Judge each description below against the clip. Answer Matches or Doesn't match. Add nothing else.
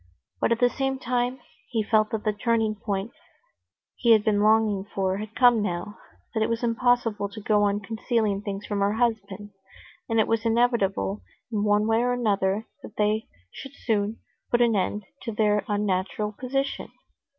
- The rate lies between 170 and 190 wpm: Matches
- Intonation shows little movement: Matches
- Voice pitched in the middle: Doesn't match